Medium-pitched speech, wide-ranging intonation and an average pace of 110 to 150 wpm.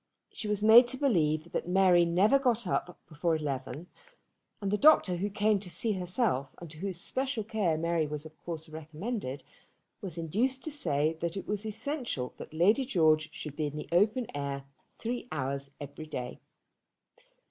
No: medium, 175 Hz; wide, 5.8 semitones; average, 175 wpm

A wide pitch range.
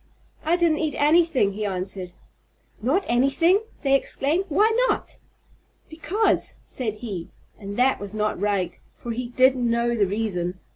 Yes: wide, 7.2 semitones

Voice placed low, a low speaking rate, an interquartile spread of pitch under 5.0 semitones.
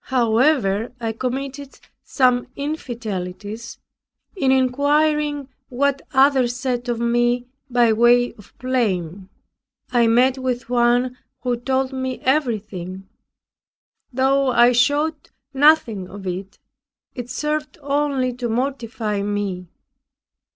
No: high, 245 Hz; slow, 105 wpm; average, 3.0 semitones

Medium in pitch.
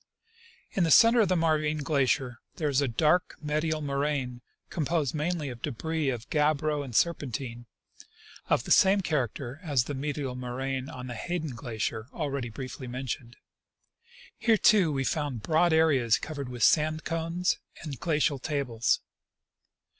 Yes: medium, 145 Hz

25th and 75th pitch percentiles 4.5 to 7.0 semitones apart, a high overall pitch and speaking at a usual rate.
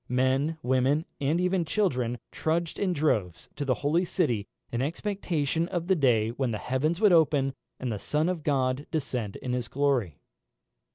No: average, 4.8 semitones; medium, 140 Hz; average, 170 wpm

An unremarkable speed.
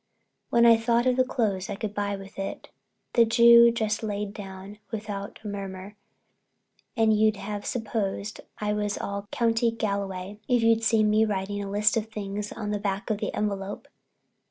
Yes: average, 180 wpm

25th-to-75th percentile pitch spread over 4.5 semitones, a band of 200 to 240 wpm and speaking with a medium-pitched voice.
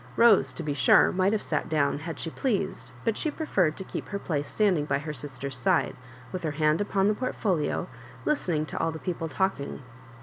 Yes: average, 4.9 semitones; fast, 205 wpm; medium, 165 Hz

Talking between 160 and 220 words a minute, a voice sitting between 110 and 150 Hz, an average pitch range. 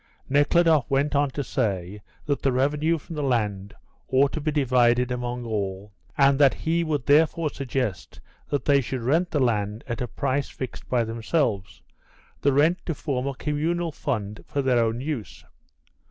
Yes: average, 170 wpm; low, 135 Hz; average, 4.0 semitones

